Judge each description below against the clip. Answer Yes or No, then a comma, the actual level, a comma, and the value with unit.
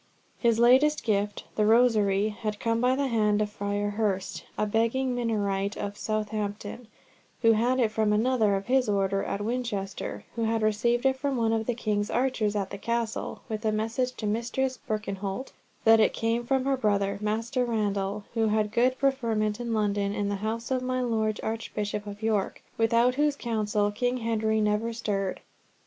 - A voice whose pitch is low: No, high, 220 Hz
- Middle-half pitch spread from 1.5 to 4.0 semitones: Yes, narrow, 2.5 semitones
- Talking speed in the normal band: Yes, average, 180 wpm